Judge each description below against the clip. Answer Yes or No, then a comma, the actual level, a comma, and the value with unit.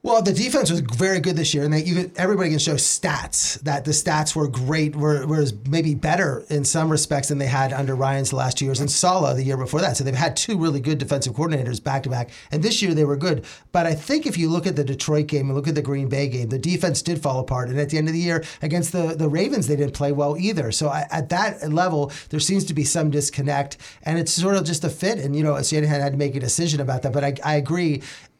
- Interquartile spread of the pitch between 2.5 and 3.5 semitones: Yes, average, 3.1 semitones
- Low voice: No, medium, 150 Hz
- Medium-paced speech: No, fast, 280 wpm